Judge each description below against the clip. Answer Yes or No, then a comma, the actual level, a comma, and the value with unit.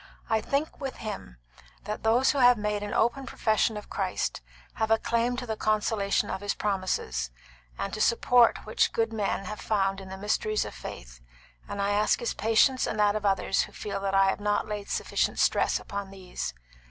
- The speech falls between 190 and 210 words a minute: Yes, average, 200 wpm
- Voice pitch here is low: No, high, 210 Hz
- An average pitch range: No, narrow, 2.2 semitones